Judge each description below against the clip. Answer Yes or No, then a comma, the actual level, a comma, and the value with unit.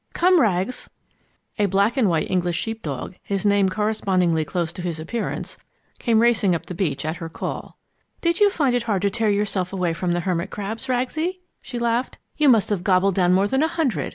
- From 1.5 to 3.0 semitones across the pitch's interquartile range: No, average, 4.8 semitones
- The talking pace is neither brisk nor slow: No, fast, 210 wpm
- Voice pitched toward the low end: No, high, 200 Hz